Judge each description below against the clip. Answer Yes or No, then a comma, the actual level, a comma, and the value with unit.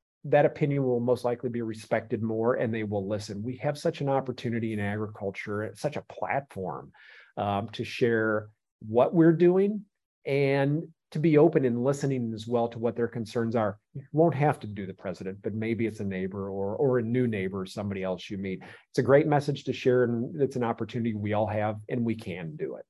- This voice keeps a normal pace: No, fast, 210 wpm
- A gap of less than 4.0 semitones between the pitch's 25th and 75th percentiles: No, average, 4.4 semitones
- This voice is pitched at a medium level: No, low, 115 Hz